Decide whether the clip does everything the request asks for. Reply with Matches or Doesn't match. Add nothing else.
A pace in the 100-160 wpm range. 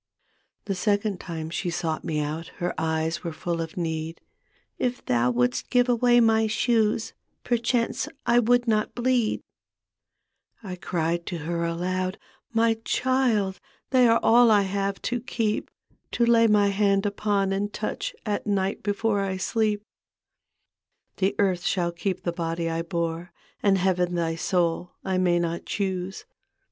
Matches